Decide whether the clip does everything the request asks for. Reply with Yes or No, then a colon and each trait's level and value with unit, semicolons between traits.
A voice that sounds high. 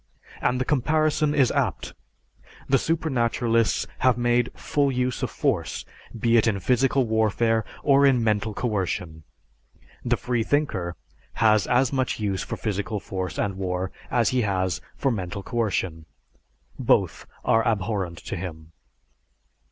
No: low, 115 Hz